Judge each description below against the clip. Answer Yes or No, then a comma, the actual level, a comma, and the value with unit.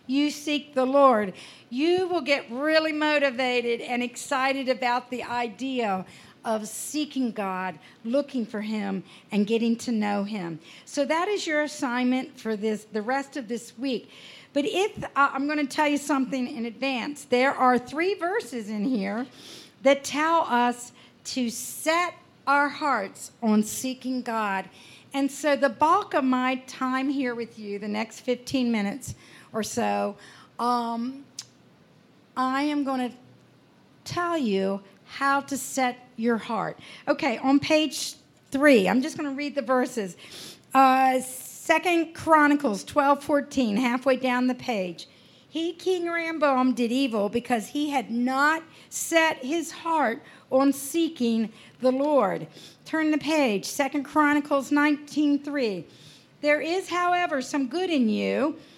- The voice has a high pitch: Yes, very high, 265 Hz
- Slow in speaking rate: No, average, 145 wpm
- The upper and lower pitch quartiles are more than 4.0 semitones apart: No, average, 3.7 semitones